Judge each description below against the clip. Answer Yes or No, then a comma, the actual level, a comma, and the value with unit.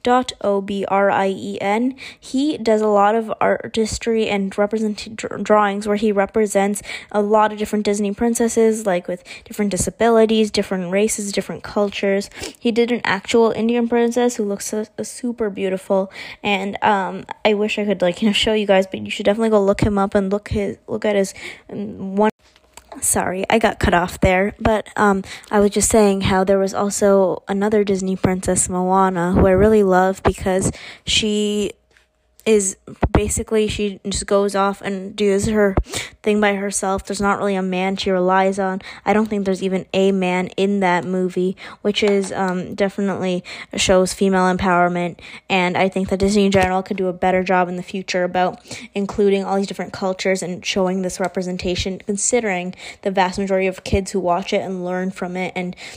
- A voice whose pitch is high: Yes, high, 200 Hz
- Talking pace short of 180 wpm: No, average, 185 wpm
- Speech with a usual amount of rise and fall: No, narrow, 2.0 semitones